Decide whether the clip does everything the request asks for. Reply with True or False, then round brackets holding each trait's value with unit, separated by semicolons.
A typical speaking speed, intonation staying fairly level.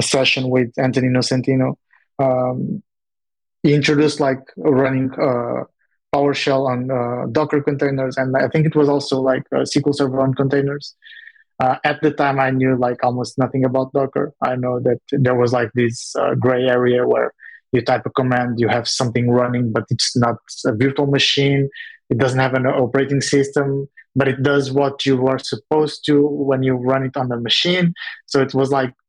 True (180 wpm; 1.9 semitones)